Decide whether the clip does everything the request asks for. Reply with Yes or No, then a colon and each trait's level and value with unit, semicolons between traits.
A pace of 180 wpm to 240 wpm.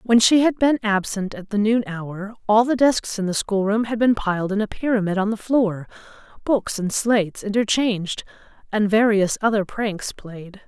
Yes: average, 185 wpm